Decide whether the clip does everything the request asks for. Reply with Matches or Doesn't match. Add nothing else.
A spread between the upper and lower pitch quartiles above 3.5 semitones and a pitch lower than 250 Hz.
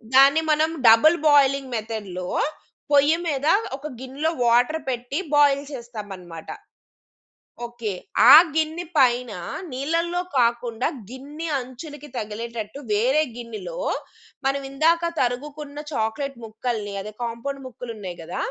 Doesn't match